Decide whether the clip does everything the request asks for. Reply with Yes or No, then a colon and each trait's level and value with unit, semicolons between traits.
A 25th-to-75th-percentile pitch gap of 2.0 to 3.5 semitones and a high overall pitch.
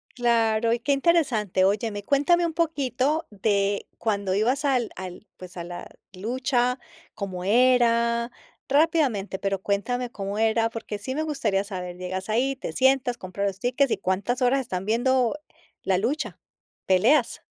No: average, 4.7 semitones; high, 230 Hz